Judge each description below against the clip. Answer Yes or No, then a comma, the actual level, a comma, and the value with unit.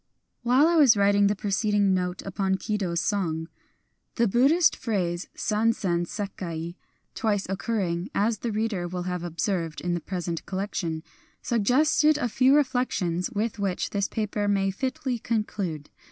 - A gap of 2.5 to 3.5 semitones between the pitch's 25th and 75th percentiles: No, average, 4.3 semitones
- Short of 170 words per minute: Yes, average, 150 wpm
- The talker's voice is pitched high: Yes, high, 200 Hz